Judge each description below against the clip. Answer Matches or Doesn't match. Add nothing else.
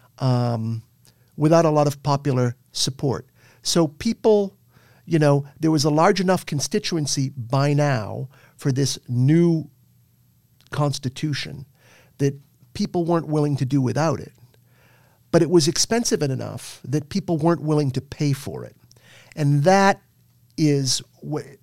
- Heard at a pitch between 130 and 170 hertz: Matches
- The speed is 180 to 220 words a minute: Doesn't match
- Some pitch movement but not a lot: Matches